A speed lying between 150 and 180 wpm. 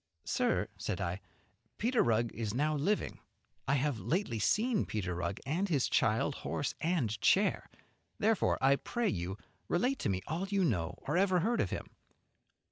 Yes: average, 170 wpm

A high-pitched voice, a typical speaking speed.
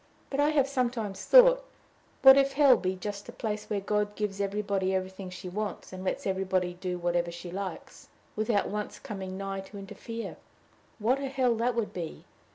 Yes: high, 205 Hz; average, 180 wpm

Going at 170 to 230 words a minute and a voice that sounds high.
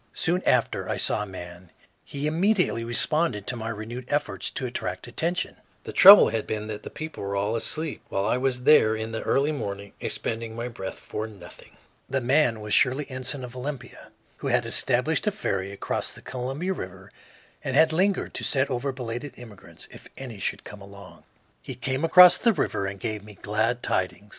No: average, 190 wpm; low, 120 Hz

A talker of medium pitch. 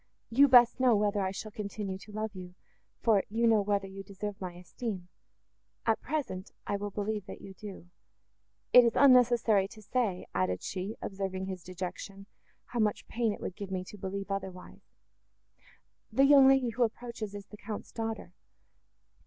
No: high, 205 Hz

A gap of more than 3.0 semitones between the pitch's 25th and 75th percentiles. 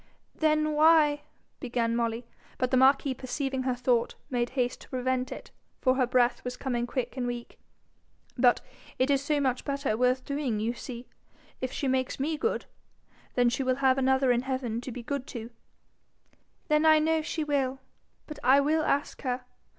No: narrow, 2.4 semitones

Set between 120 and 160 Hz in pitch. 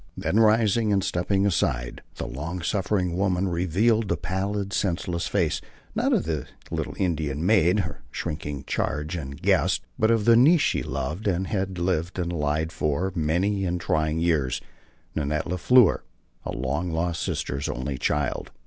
No: very low, 90 Hz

